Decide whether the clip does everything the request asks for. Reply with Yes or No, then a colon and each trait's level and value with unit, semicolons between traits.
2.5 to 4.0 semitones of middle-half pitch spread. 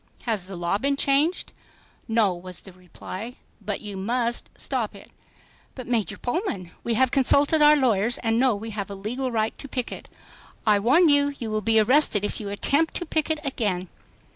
No: wide, 5.4 semitones